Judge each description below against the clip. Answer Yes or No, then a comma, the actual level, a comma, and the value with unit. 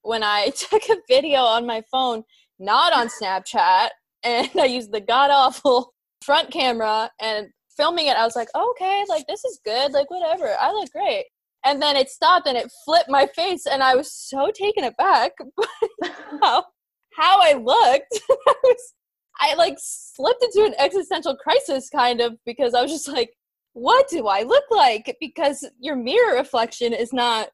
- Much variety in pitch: Yes, wide, 8.0 semitones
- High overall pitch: Yes, very high, 285 Hz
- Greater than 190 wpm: No, average, 180 wpm